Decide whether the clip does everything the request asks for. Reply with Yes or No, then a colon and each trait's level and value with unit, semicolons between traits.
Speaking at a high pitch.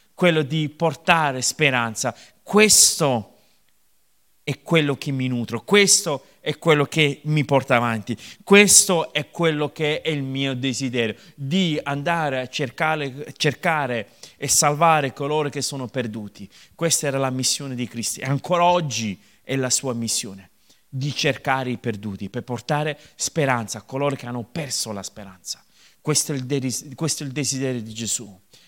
No: medium, 140 Hz